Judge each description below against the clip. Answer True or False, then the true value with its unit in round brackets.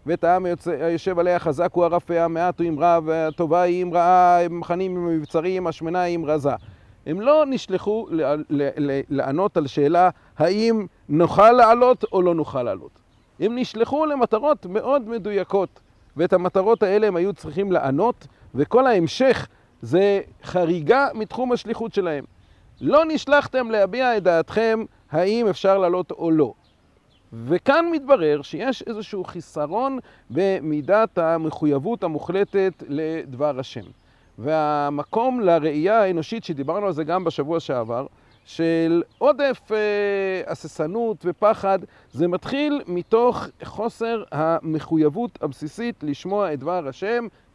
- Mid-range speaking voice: True (180 Hz)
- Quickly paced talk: False (130 wpm)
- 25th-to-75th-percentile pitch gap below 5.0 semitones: False (5.4 semitones)